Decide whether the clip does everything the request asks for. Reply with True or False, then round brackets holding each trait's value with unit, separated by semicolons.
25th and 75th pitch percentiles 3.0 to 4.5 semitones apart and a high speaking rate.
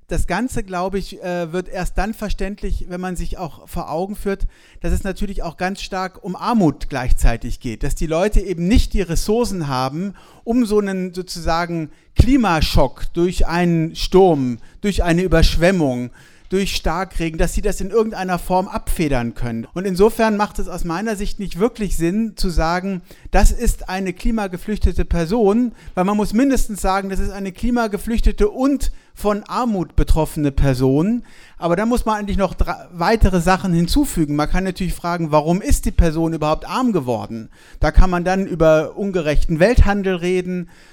False (3.6 semitones; 165 wpm)